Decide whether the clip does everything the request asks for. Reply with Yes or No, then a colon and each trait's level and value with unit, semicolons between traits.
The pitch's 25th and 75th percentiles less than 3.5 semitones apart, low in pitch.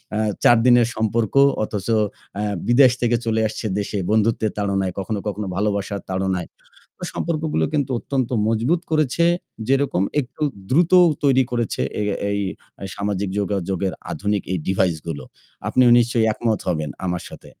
No: average, 4.2 semitones; low, 110 Hz